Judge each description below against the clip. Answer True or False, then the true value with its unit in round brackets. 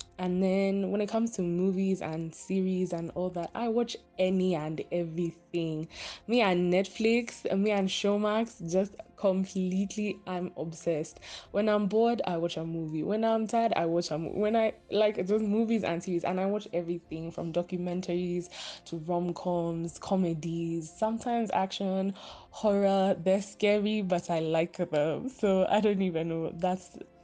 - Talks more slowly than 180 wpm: True (160 wpm)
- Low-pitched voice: False (185 Hz)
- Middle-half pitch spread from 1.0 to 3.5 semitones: True (3.2 semitones)